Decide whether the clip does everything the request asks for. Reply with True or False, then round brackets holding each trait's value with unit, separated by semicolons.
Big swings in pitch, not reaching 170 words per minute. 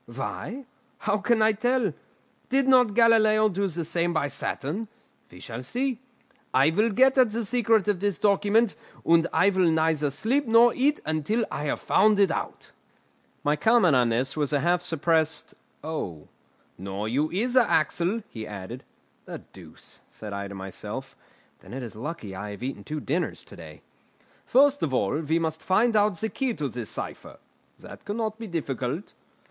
False (7.8 semitones; 175 wpm)